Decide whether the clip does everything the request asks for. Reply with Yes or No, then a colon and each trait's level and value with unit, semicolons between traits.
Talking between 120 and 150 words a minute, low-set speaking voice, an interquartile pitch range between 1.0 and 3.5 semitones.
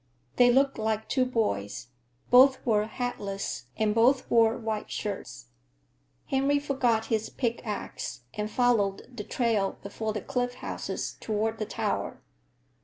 No: slow, 135 wpm; high, 225 Hz; average, 2.9 semitones